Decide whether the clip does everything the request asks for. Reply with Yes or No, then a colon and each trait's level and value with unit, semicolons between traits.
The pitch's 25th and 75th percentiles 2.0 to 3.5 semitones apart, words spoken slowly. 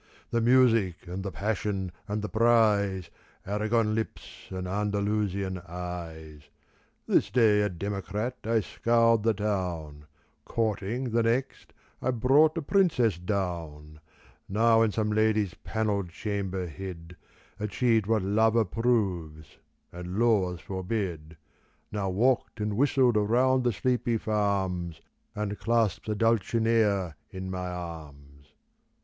No: average, 3.9 semitones; slow, 120 wpm